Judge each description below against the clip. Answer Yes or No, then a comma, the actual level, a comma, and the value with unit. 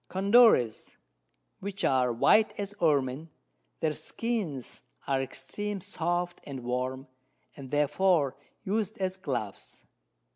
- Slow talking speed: Yes, slow, 105 wpm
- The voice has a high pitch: No, medium, 160 Hz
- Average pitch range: No, wide, 6.8 semitones